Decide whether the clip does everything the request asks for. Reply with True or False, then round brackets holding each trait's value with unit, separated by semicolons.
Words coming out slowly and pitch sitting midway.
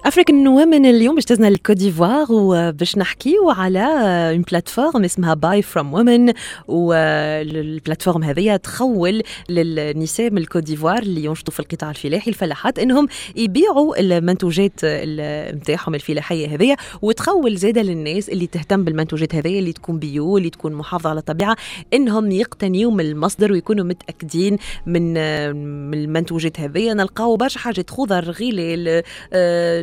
True (125 wpm; 180 Hz)